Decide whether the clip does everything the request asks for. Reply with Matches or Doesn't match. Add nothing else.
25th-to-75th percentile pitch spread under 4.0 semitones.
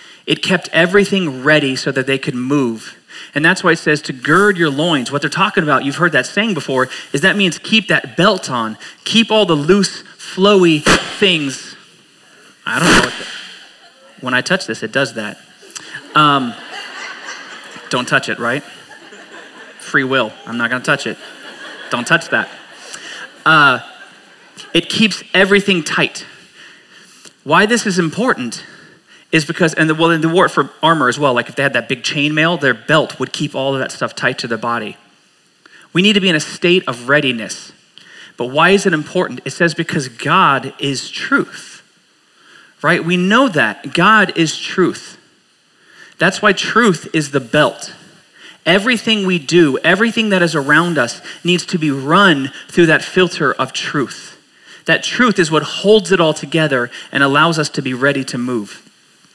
Doesn't match